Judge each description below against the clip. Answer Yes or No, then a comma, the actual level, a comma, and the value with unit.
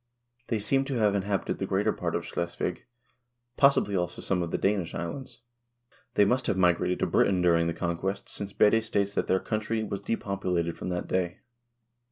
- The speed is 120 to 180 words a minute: No, average, 190 wpm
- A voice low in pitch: Yes, low, 100 Hz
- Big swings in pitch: No, average, 3.4 semitones